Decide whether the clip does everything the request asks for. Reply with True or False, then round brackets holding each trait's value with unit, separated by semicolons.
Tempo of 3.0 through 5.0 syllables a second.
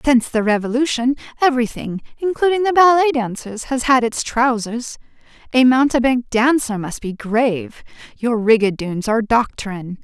False (5.2 syllables/s)